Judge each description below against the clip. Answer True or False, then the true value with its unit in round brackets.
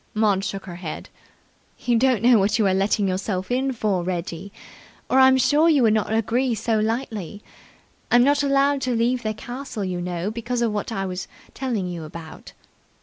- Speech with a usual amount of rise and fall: True (4.6 semitones)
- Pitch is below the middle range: False (220 Hz)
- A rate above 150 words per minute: True (185 wpm)